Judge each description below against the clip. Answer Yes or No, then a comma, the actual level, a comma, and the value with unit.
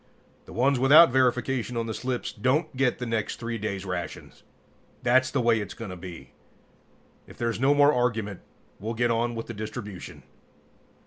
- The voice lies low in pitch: Yes, low, 120 Hz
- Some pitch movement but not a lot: Yes, average, 3.0 semitones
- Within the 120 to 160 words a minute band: No, average, 175 wpm